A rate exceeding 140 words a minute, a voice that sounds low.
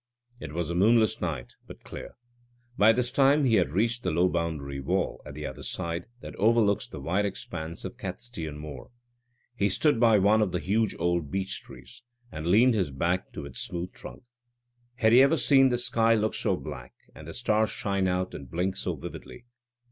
Yes: average, 195 wpm; very low, 95 Hz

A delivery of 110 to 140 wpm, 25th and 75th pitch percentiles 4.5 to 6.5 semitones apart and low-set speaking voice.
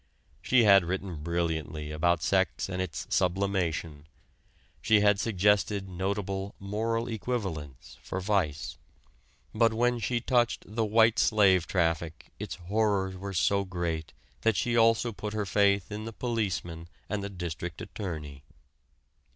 No: slow, 135 wpm; average, 3.9 semitones; very low, 95 Hz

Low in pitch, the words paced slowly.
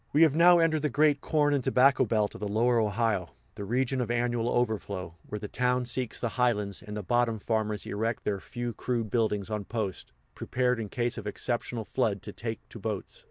No: low, 115 Hz; fast, 205 wpm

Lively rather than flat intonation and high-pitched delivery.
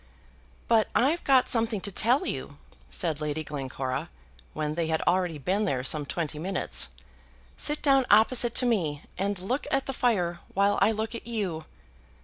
Yes: wide, 6.8 semitones; high, 195 Hz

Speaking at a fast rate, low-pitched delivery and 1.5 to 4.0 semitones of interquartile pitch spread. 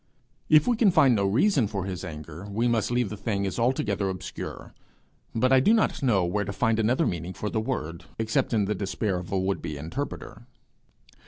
No: fast, 210 wpm; low, 105 Hz; average, 4.6 semitones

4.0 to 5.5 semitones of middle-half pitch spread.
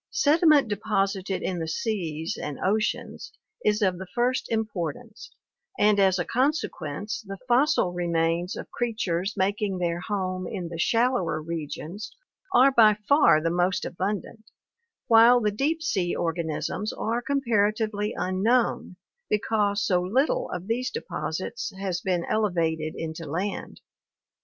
Yes: average, 4.5 semitones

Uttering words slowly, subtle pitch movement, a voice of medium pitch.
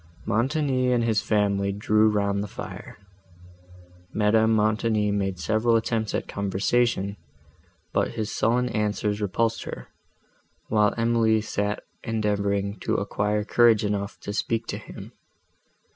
No: slow, 125 wpm; narrow, 1.9 semitones; low, 105 Hz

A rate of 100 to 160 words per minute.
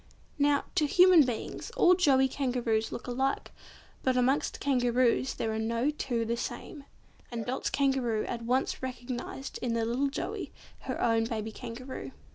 Yes: average, 155 wpm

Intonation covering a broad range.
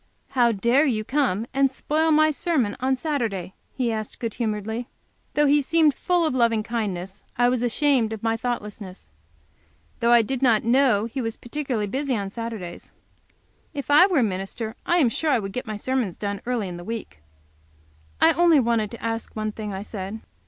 No: average, 4.2 semitones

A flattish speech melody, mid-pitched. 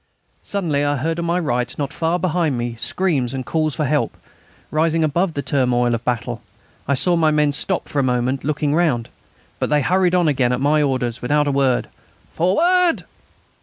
No: average, 4.3 semitones; medium, 145 Hz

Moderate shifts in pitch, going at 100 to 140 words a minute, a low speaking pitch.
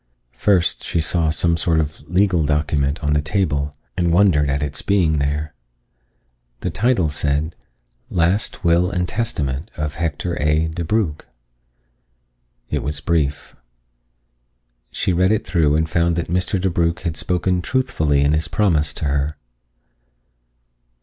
Yes: average, 3.2 semitones; slow, 135 wpm; very low, 80 Hz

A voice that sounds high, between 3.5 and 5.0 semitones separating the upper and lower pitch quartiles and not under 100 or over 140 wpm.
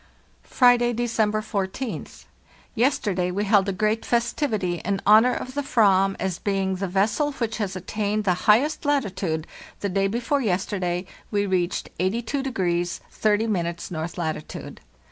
Yes: high, 205 Hz; average, 4.0 semitones; slow, 135 wpm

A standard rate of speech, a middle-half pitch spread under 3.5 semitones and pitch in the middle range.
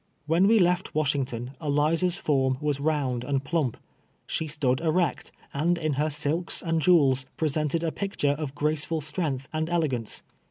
Yes: average, 155 wpm; average, 2.9 semitones; medium, 150 Hz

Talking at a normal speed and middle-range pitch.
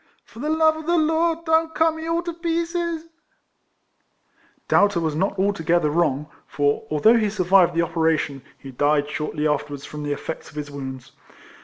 Yes: average, 175 wpm; medium, 175 Hz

